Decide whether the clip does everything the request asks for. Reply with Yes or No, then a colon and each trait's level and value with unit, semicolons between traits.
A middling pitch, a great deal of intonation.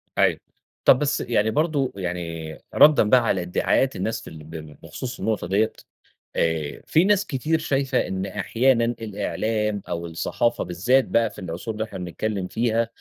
No: low, 110 Hz; wide, 5.8 semitones